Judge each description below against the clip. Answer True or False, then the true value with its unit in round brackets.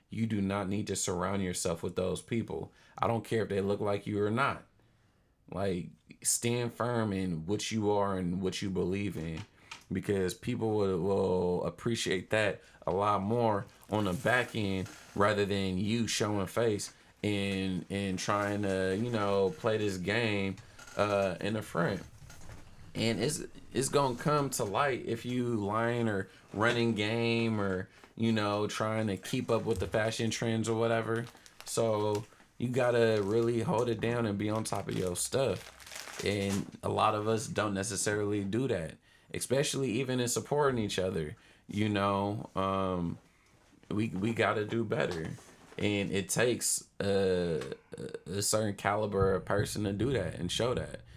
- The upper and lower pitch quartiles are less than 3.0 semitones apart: True (2.6 semitones)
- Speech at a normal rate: True (165 wpm)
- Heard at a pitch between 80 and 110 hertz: True (105 Hz)